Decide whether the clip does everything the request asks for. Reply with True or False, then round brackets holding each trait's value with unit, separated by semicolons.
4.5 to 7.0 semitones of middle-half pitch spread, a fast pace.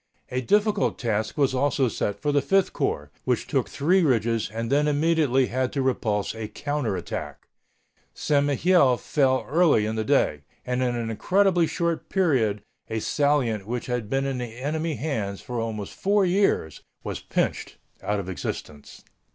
False (5.1 semitones; 165 wpm)